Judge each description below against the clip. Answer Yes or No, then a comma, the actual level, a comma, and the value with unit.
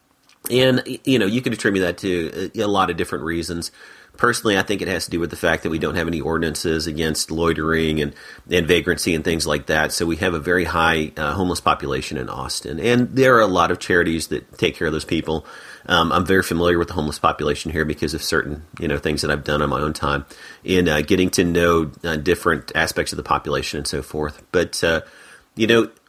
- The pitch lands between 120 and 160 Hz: No, very low, 85 Hz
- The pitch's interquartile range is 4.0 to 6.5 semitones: No, average, 3.1 semitones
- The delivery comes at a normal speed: No, fast, 235 wpm